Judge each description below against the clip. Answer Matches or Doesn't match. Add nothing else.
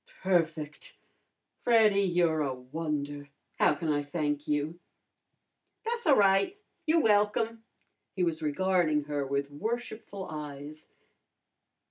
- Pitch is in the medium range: Matches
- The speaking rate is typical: Doesn't match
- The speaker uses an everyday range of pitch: Doesn't match